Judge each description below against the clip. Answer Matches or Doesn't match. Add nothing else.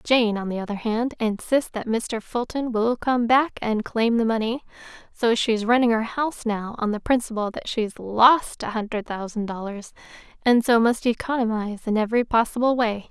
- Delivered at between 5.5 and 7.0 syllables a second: Doesn't match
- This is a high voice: Matches